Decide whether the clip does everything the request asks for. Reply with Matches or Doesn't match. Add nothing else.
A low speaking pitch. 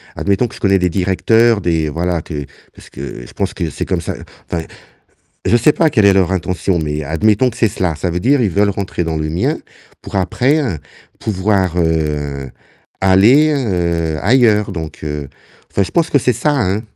Matches